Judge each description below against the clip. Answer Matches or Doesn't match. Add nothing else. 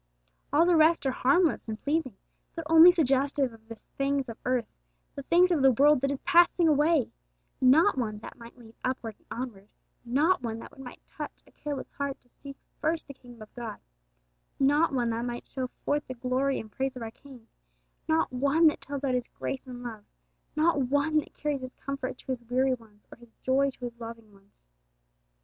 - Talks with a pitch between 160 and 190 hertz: Doesn't match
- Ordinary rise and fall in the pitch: Matches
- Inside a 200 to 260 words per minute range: Matches